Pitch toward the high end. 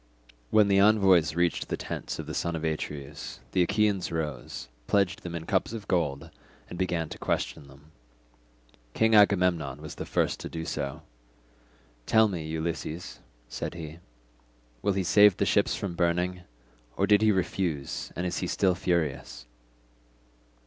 No: very low, 85 Hz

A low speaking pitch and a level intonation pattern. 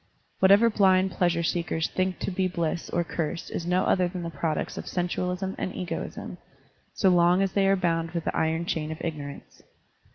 No: medium, 175 Hz; narrow, 2.0 semitones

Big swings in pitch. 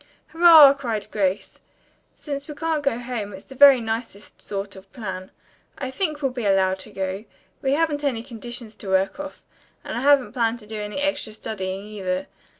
Yes: wide, 5.9 semitones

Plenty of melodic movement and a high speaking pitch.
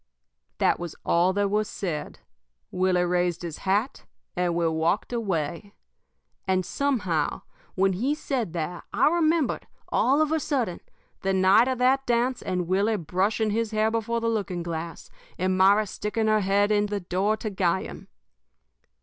No: average, 4.2 semitones; high, 200 Hz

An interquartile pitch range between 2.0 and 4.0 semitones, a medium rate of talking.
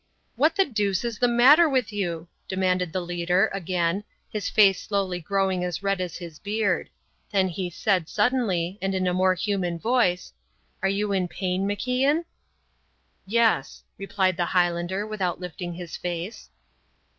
Yes: average, 2.9 semitones; average, 155 wpm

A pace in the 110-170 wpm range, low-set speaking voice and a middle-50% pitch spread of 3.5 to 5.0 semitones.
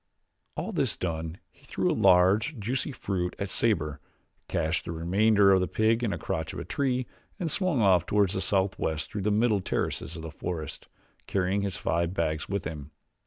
No: average, 190 wpm; very low, 95 Hz; average, 4.3 semitones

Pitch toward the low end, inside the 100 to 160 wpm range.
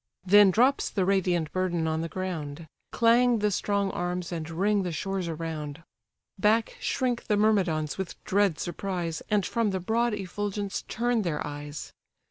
No: high, 190 Hz; average, 155 wpm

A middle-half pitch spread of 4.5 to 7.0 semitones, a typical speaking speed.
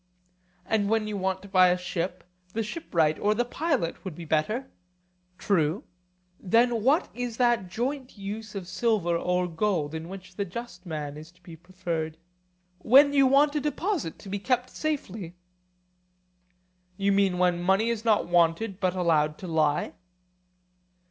Yes: average, 5.1 semitones; average, 160 wpm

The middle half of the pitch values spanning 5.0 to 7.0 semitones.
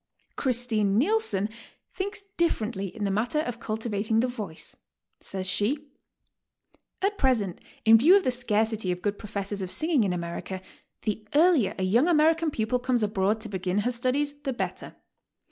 Yes: wide, 5.6 semitones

